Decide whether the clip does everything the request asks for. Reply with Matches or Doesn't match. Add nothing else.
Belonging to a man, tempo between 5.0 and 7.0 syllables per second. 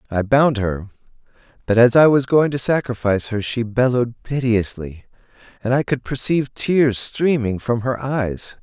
Doesn't match